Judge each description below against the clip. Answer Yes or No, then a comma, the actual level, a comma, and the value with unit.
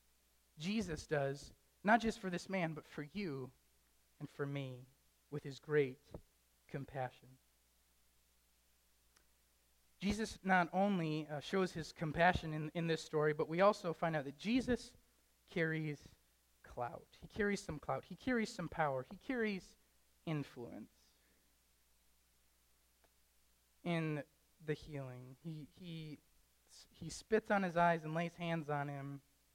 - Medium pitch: Yes, medium, 145 Hz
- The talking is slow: Yes, slow, 130 wpm